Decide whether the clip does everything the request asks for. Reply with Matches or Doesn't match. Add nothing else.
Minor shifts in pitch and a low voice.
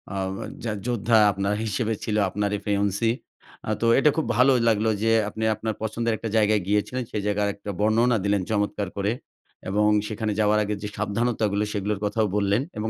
Matches